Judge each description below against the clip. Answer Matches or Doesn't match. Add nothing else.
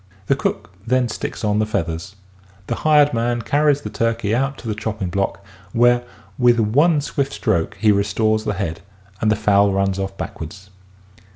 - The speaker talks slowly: Doesn't match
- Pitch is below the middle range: Matches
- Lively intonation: Doesn't match